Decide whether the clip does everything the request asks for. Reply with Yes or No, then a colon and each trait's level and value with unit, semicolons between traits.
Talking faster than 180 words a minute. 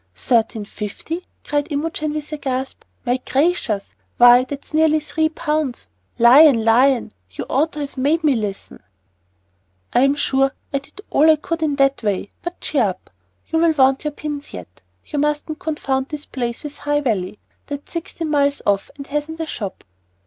No: average, 170 wpm